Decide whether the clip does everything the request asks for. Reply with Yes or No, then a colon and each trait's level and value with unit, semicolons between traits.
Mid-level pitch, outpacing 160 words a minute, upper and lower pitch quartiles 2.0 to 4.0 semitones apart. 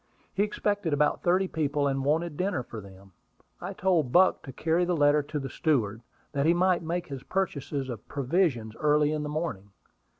No: medium, 150 Hz; average, 190 wpm; average, 4.5 semitones